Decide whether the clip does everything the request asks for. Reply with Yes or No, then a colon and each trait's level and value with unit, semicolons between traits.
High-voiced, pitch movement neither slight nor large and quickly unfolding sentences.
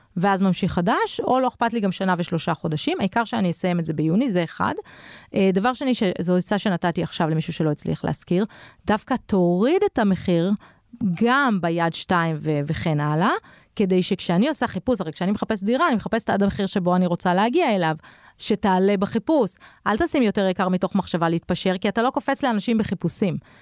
Yes: high, 195 Hz; average, 4.3 semitones; fast, 180 wpm